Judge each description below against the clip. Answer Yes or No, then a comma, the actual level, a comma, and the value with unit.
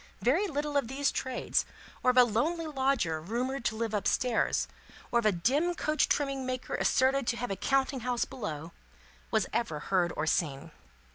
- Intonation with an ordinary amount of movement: Yes, average, 4.7 semitones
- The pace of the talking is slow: No, average, 185 wpm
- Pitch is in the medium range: No, very high, 250 Hz